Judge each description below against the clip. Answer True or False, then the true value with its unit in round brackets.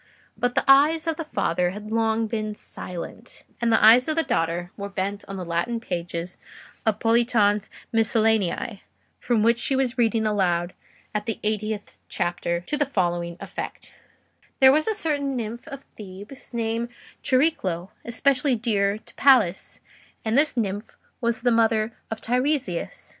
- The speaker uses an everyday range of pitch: True (3.9 semitones)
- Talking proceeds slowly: False (155 wpm)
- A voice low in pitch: False (225 Hz)